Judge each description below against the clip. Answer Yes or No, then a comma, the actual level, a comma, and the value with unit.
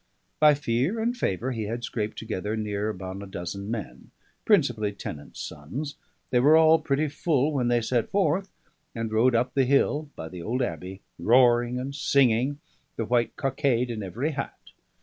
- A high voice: No, low, 120 Hz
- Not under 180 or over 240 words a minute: No, average, 170 wpm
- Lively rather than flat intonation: No, average, 4.5 semitones